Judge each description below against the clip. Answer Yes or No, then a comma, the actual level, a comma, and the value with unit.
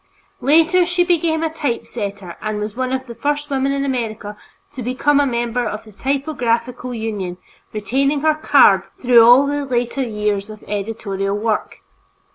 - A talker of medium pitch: No, high, 245 Hz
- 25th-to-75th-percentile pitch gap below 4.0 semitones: No, average, 4.7 semitones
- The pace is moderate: Yes, average, 160 wpm